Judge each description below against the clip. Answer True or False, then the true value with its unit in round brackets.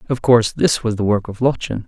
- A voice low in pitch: True (115 Hz)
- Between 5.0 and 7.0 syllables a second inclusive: True (6.0 syllables/s)